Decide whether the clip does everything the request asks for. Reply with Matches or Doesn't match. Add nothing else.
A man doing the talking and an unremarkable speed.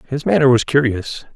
Matches